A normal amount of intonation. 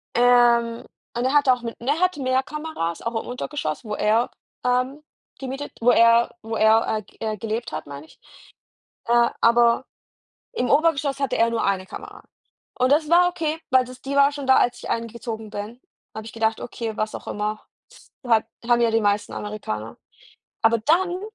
Yes: average, 3.6 semitones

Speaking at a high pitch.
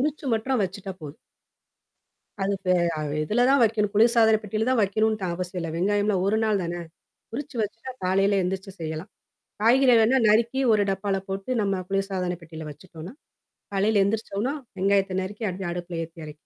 Yes: high, 200 Hz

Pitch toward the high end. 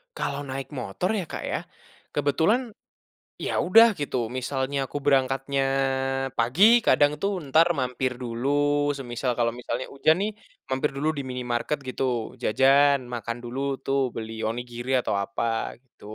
No: low, 130 Hz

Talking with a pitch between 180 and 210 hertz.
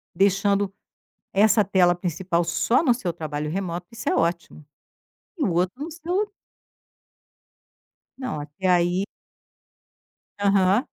Yes: high, 190 Hz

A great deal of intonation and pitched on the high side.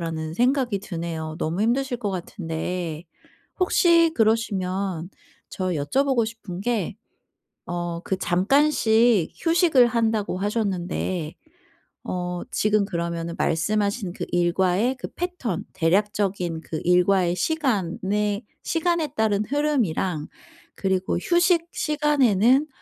Yes: wide, 5.7 semitones; high, 200 Hz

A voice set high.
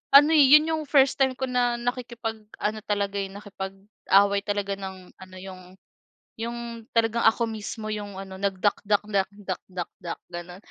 Yes: high, 205 Hz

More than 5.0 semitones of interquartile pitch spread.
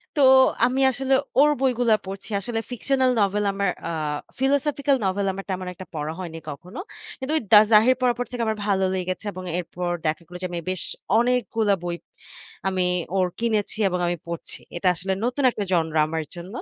Yes: wide, 5.4 semitones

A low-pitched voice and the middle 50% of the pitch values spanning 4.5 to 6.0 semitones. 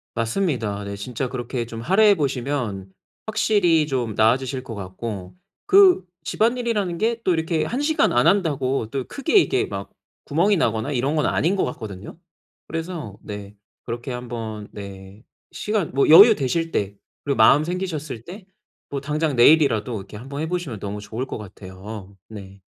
No: low, 130 Hz; wide, 7.7 semitones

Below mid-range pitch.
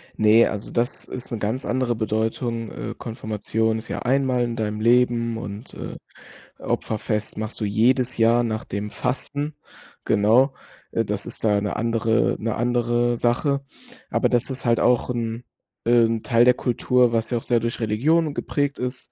Yes: low, 115 Hz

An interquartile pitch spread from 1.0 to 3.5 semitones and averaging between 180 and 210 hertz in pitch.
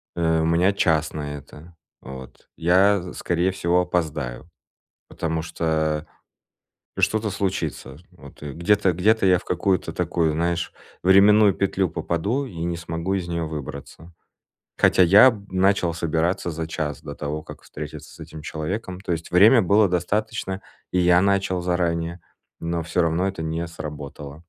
No: average, 3.0 semitones; very low, 85 Hz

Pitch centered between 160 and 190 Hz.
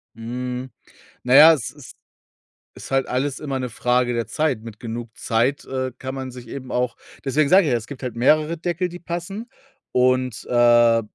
No: low, 130 Hz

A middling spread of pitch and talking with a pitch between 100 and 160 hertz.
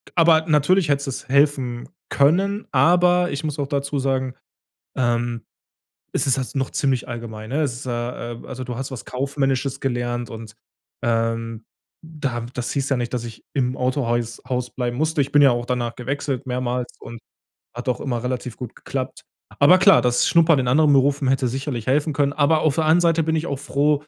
Yes: average, 3.2 semitones; low, 135 Hz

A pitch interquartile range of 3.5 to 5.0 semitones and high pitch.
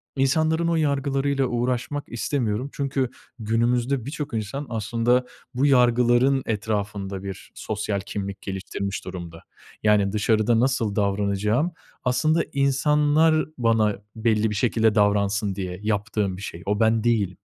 No: average, 4.7 semitones; low, 115 Hz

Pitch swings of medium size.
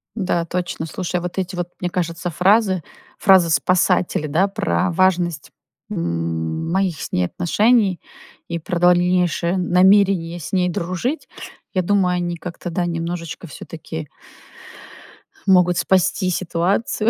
No: narrow, 1.9 semitones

